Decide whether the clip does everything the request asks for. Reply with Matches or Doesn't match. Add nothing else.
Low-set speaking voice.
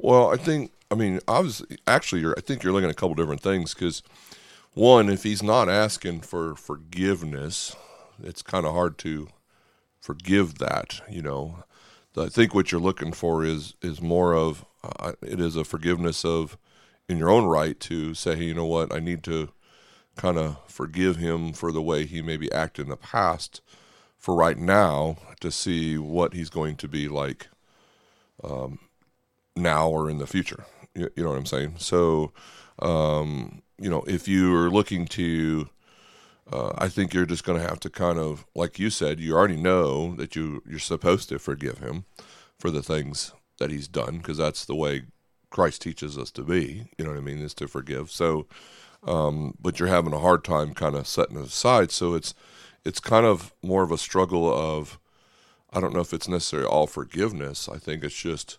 Matches